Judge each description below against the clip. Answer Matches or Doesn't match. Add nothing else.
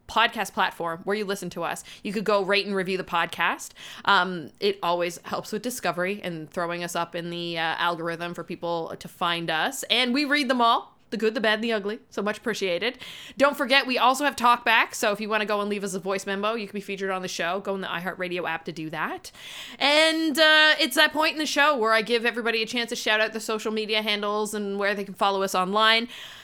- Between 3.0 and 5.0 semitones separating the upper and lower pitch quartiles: Matches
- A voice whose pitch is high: Matches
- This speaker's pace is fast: Matches